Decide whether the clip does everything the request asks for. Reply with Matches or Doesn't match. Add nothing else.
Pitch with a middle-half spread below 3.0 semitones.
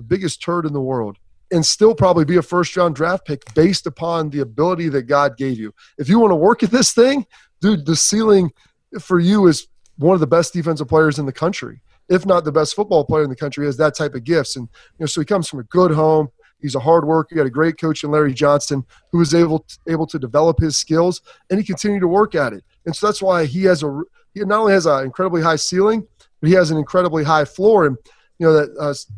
Doesn't match